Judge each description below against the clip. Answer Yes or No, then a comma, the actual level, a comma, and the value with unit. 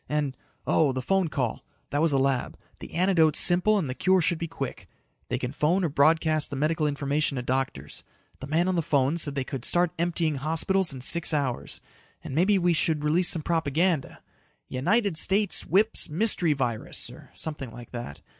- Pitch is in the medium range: Yes, medium, 155 Hz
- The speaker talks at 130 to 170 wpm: No, average, 190 wpm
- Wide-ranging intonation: No, average, 4.2 semitones